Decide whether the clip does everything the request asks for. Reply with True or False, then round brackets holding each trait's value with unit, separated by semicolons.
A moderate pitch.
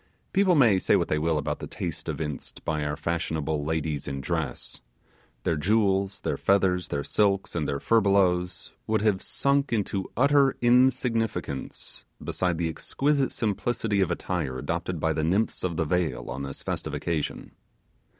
False (90 Hz)